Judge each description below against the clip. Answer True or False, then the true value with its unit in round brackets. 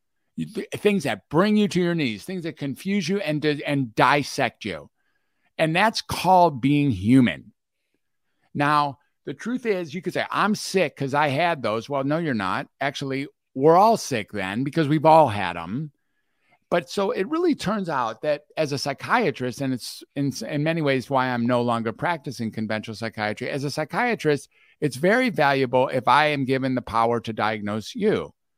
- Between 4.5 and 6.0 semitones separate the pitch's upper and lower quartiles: True (5.1 semitones)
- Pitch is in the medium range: True (145 Hz)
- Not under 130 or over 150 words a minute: False (180 wpm)